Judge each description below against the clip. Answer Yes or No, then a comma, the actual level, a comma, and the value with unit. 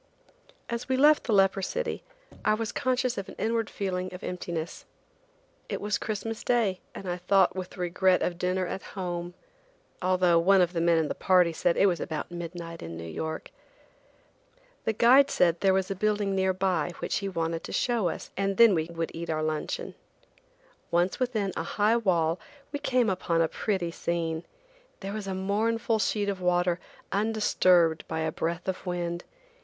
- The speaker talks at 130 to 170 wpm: No, average, 180 wpm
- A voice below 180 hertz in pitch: No, medium, 185 Hz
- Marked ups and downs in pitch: No, average, 3.4 semitones